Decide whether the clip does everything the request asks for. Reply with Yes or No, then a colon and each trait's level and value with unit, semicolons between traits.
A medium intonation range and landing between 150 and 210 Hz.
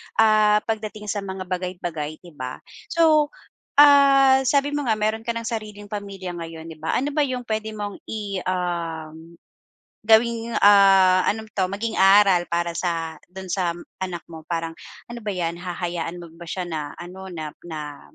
Yes: average, 4.3 semitones; high, 190 Hz